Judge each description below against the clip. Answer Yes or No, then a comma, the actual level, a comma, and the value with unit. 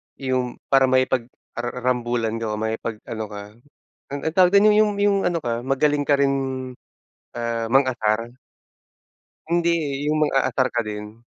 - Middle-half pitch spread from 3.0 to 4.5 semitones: Yes, average, 3.8 semitones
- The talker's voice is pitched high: No, low, 130 Hz